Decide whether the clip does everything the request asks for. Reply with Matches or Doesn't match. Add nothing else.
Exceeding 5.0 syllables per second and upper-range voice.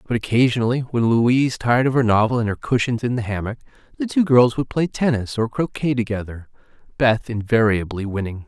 Doesn't match